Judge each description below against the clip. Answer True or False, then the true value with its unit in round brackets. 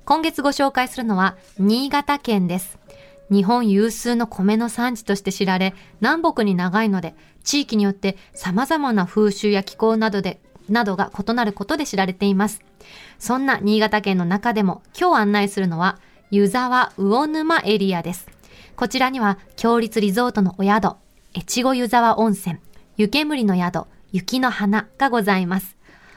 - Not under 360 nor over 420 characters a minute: False (295 characters per minute)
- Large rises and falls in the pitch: False (3.9 semitones)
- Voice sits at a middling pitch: False (210 Hz)